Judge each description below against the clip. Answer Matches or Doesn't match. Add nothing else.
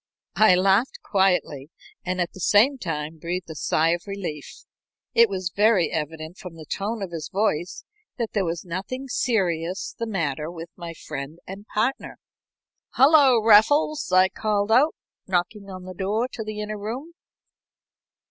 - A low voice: Doesn't match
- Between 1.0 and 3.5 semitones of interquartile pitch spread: Doesn't match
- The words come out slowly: Doesn't match